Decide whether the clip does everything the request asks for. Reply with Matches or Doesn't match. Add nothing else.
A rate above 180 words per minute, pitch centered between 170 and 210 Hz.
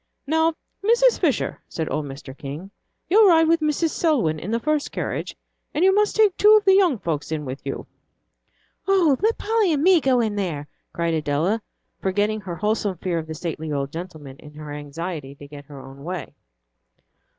Matches